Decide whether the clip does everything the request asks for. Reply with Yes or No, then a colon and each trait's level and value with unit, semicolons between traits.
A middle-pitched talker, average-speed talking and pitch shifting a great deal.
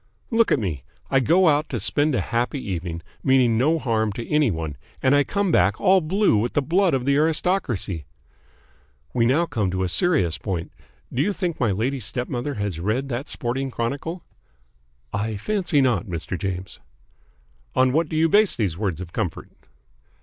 No: low, 125 Hz; average, 180 wpm; wide, 7.4 semitones